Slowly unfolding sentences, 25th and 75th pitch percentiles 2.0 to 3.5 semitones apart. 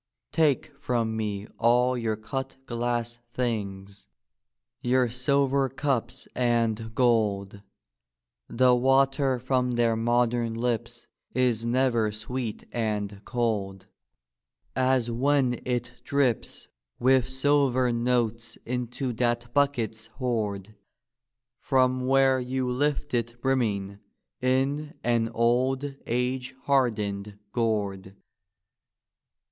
Yes: slow, 95 wpm; narrow, 2.5 semitones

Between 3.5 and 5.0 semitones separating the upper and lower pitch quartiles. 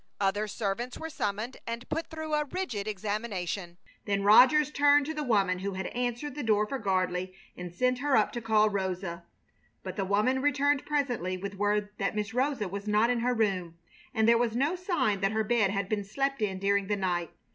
Yes: average, 4.7 semitones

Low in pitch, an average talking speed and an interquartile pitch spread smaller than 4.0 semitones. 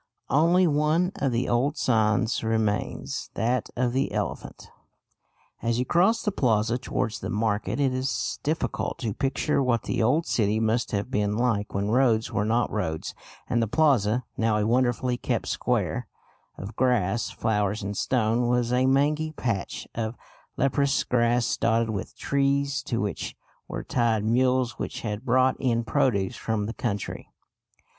Yes: low, 120 Hz; average, 155 wpm; average, 3.2 semitones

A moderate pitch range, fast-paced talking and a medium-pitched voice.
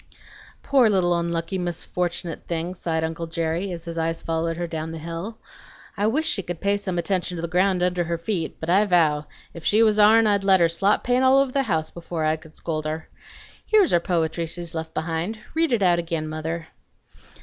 Yes: average, 3.4 semitones; fast, 210 wpm; medium, 170 Hz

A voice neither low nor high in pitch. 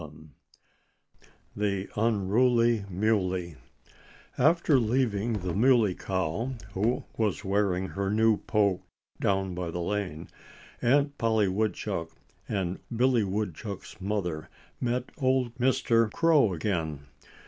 No: low, 105 Hz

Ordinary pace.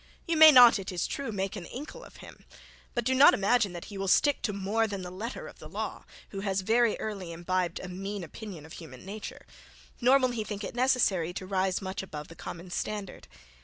No: fast, 225 wpm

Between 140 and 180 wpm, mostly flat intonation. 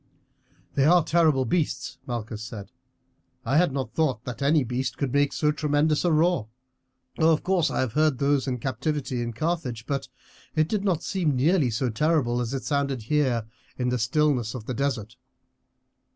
No: average, 175 wpm; average, 4.0 semitones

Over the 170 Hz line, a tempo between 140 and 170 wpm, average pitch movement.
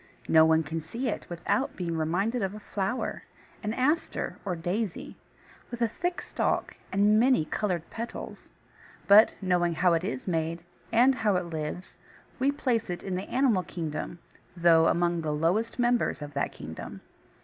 No: medium, 185 Hz; average, 165 wpm; wide, 5.7 semitones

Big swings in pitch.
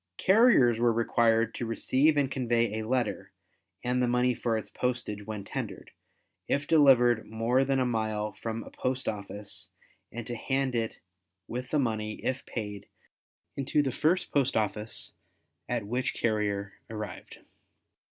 No: average, 3.1 semitones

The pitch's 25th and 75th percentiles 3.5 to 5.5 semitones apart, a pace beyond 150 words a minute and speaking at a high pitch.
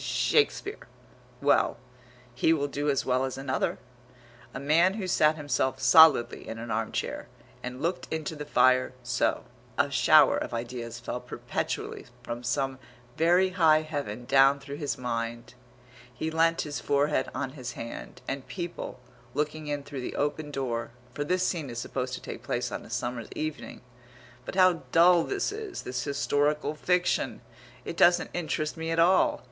No: average, 4.3 semitones; average, 165 wpm; medium, 145 Hz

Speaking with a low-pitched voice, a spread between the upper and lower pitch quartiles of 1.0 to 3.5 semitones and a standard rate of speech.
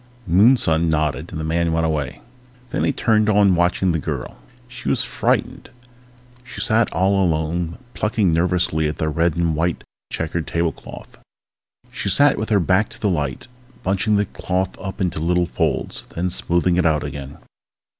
Yes: very low, 85 Hz; average, 3.2 semitones; average, 165 wpm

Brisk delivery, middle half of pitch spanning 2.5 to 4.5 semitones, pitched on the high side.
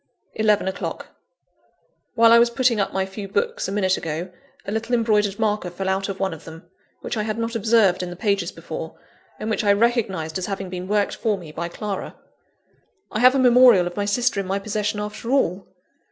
Yes: fast, 210 wpm; average, 3.2 semitones; high, 205 Hz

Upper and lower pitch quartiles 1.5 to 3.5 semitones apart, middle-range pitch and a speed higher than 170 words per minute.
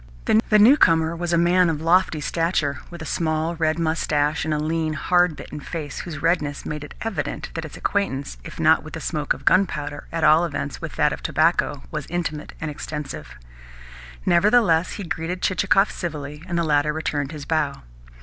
Yes: narrow, 2.6 semitones; medium, 160 Hz; average, 185 wpm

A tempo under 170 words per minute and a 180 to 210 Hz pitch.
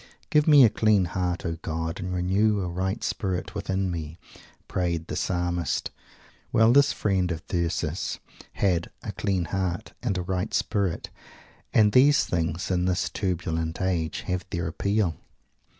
No: average, 150 wpm; very low, 90 Hz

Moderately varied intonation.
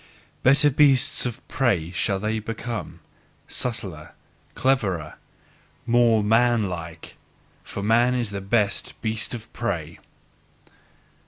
Yes: average, 3.7 semitones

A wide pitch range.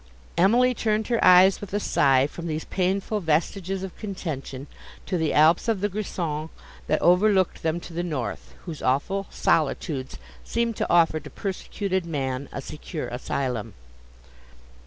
No: average, 4.8 semitones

